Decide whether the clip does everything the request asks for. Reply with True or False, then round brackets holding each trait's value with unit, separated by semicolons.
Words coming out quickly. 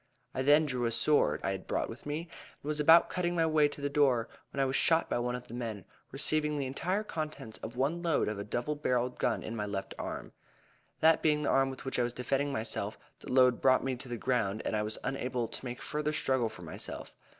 True (245 wpm)